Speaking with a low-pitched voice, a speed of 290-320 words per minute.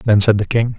Yes: low, 110 Hz; fast, 305 wpm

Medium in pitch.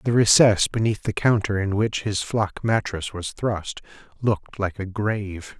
No: low, 105 Hz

